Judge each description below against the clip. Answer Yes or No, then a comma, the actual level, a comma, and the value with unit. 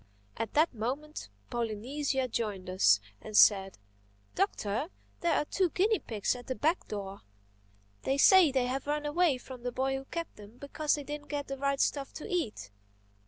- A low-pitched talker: No, very high, 270 Hz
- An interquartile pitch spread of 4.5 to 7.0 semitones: Yes, average, 5.2 semitones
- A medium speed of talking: Yes, average, 175 wpm